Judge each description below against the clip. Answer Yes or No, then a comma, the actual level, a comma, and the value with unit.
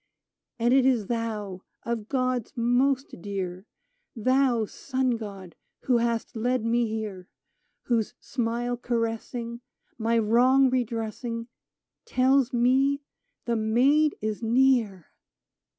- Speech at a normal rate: No, slow, 115 wpm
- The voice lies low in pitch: No, high, 235 Hz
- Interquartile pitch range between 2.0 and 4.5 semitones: Yes, narrow, 2.6 semitones